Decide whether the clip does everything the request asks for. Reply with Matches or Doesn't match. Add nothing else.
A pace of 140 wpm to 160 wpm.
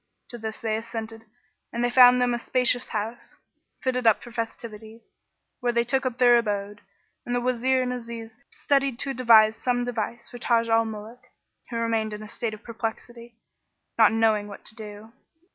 Doesn't match